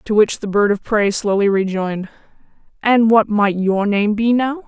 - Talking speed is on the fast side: No, average, 195 wpm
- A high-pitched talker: Yes, high, 210 Hz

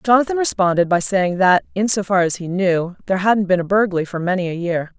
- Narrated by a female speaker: Yes, female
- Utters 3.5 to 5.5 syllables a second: No, 6.0 syllables/s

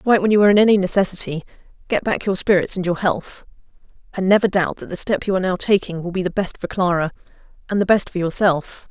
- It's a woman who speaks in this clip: Yes, female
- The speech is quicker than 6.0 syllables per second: Yes, 6.6 syllables/s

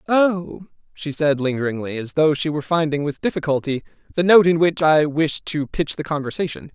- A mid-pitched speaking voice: Yes, medium, 155 Hz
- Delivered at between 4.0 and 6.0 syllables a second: Yes, 5.4 syllables/s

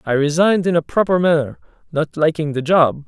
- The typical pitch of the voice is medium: Yes, medium, 155 Hz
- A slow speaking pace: No, average, 195 wpm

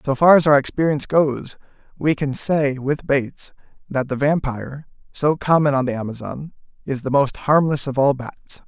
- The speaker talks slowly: No, average, 180 wpm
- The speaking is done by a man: Yes, male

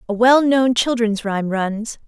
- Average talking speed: Yes, average, 145 wpm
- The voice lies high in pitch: Yes, high, 230 Hz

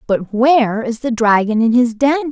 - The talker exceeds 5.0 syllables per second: No, 4.9 syllables/s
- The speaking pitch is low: No, high, 240 Hz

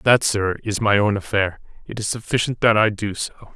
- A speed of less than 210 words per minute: No, fast, 220 wpm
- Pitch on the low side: Yes, low, 105 Hz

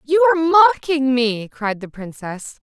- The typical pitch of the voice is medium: No, very high, 275 Hz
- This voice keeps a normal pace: Yes, average, 155 wpm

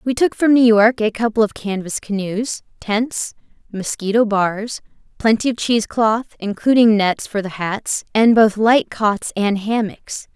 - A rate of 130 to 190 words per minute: Yes, average, 155 wpm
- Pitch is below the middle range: No, high, 220 Hz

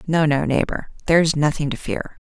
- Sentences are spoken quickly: No, average, 185 wpm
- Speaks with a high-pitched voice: No, medium, 155 Hz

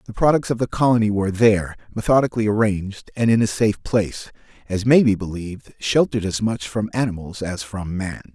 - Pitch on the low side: Yes, low, 105 Hz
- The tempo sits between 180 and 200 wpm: Yes, average, 185 wpm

